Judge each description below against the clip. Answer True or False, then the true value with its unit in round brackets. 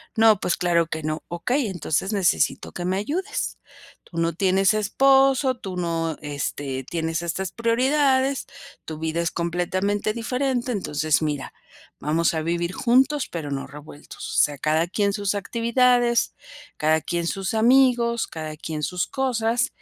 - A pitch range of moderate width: False (6.6 semitones)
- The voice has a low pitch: False (185 Hz)